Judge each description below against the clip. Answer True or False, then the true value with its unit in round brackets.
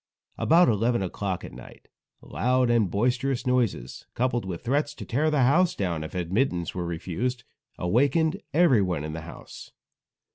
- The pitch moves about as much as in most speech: False (6.9 semitones)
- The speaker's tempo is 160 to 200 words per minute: False (150 wpm)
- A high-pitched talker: False (120 Hz)